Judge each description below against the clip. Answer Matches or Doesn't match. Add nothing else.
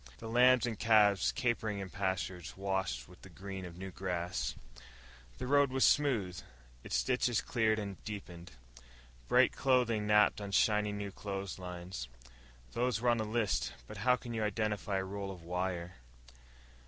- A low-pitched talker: Matches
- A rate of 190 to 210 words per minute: Doesn't match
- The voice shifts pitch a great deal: Doesn't match